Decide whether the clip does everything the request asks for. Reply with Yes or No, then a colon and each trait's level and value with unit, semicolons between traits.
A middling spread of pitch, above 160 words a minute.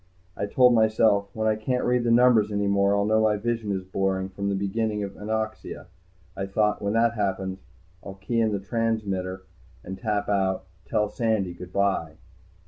No: narrow, 2.2 semitones; average, 185 wpm